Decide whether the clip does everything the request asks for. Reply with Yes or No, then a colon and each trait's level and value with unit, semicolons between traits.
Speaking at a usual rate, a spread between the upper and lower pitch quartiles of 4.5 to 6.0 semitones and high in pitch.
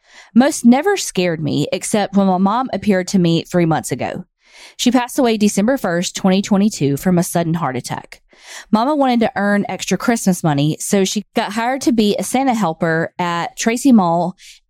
Yes: average, 180 wpm; average, 5.0 semitones; high, 195 Hz